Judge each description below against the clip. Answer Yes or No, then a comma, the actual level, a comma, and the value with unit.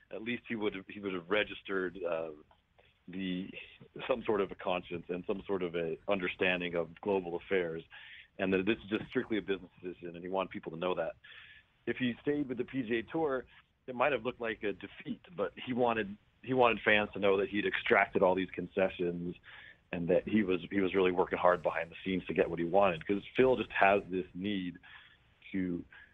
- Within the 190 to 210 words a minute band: Yes, fast, 205 wpm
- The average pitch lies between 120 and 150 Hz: No, low, 100 Hz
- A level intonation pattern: No, average, 3.3 semitones